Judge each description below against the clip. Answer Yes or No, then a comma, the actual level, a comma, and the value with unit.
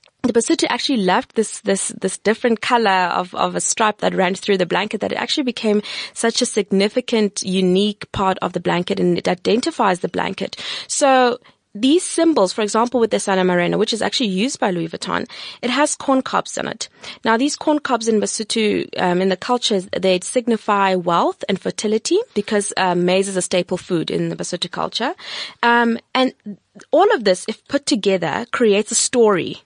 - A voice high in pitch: Yes, high, 215 Hz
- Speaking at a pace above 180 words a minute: Yes, average, 190 wpm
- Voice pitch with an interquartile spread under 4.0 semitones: No, average, 4.5 semitones